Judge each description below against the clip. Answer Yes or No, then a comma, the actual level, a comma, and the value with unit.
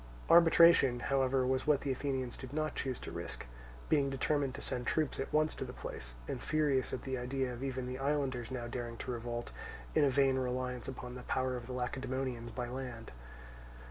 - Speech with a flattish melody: Yes, narrow, 1.8 semitones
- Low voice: Yes, low, 130 Hz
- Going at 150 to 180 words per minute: No, average, 200 wpm